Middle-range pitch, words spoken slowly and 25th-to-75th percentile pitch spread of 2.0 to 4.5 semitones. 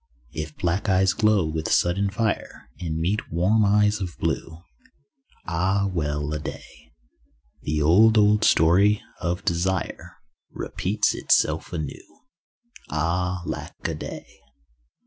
No: very low, 90 Hz; slow, 120 wpm; average, 3.8 semitones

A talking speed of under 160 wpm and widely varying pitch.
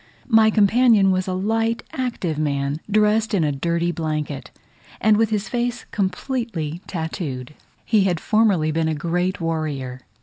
Yes: average, 145 wpm; wide, 5.7 semitones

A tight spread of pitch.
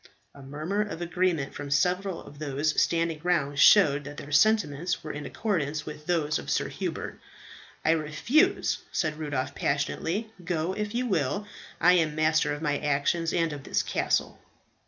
No: average, 3.6 semitones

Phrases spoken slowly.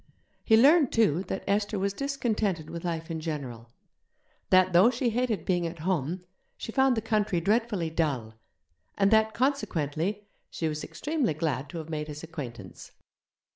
No: average, 160 wpm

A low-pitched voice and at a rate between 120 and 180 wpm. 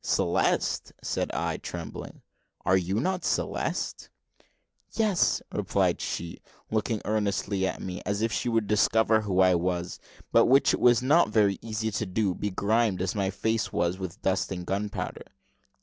Yes: low, 105 Hz; average, 155 wpm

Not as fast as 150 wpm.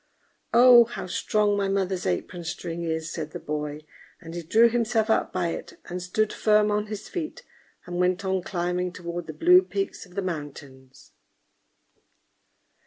No: average, 165 wpm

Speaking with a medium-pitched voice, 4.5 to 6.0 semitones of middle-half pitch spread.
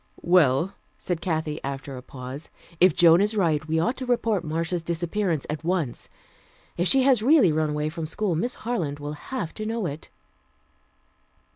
Yes: medium, 165 Hz; average, 5.1 semitones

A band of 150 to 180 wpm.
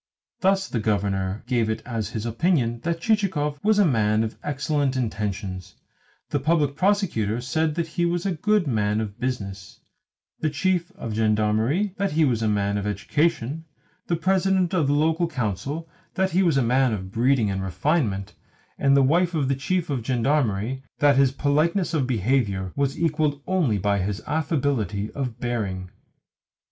Yes: average, 165 wpm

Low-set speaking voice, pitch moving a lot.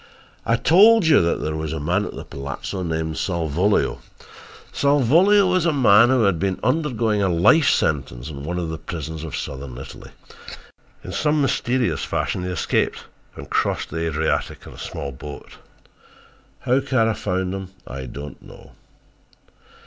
Yes: very low, 90 Hz; wide, 8.5 semitones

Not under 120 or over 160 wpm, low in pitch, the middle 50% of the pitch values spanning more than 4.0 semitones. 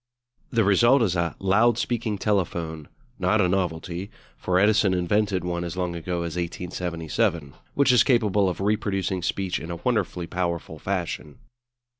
No: average, 150 wpm; very low, 90 Hz; average, 3.3 semitones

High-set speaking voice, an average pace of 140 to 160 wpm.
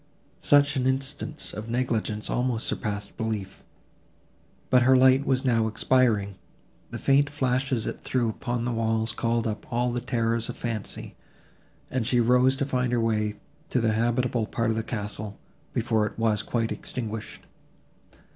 No: low, 115 Hz; average, 155 wpm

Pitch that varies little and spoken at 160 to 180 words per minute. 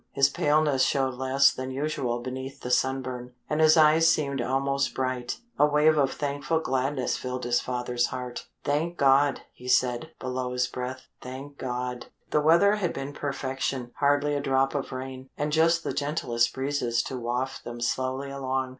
Yes: narrow, 2.2 semitones; average, 170 wpm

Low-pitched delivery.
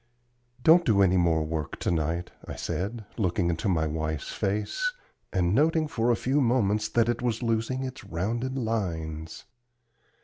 Yes: low, 105 Hz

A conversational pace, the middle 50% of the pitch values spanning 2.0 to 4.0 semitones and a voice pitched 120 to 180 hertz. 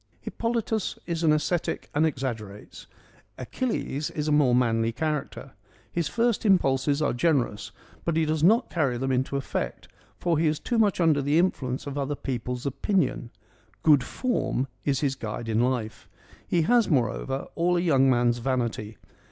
No: average, 170 wpm; average, 4.9 semitones; medium, 140 Hz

